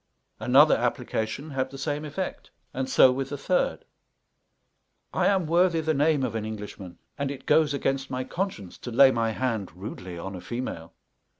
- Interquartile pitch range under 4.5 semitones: No, average, 5.2 semitones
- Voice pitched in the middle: No, low, 130 Hz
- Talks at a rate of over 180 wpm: No, average, 175 wpm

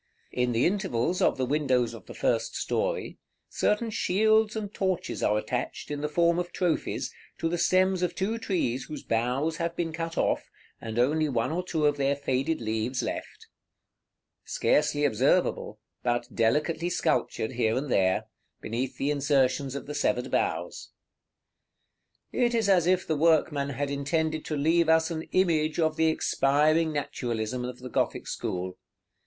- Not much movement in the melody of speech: No, average, 5.1 semitones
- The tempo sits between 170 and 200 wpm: No, average, 160 wpm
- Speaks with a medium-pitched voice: Yes, medium, 150 Hz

